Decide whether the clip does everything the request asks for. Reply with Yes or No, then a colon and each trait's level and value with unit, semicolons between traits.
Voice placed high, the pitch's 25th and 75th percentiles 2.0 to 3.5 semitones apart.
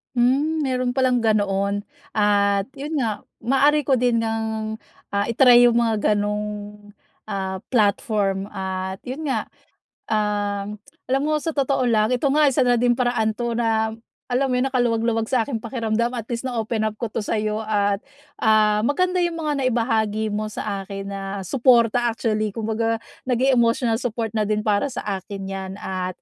Yes: high, 225 Hz; average, 3.0 semitones